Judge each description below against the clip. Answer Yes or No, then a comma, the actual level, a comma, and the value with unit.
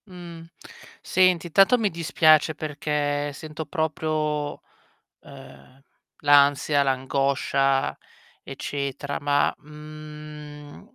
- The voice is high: No, medium, 150 Hz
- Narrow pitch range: Yes, narrow, 1.7 semitones